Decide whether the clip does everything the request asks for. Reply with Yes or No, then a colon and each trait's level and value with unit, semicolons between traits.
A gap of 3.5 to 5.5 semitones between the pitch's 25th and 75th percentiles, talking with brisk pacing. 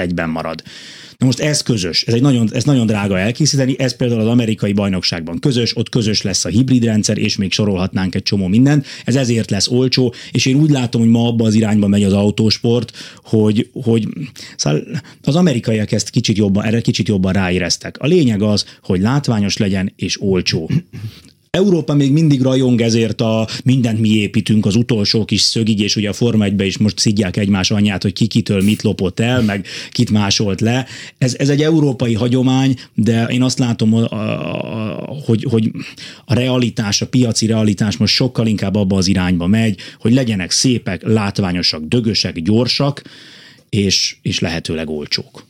Yes: average, 3.8 semitones; fast, 175 wpm